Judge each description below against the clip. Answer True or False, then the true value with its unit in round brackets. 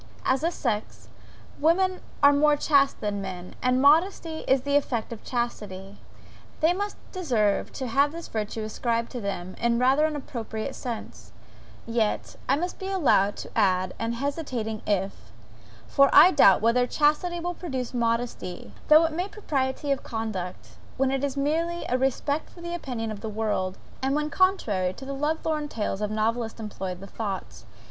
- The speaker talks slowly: False (170 wpm)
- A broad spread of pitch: True (5.7 semitones)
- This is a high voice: True (255 Hz)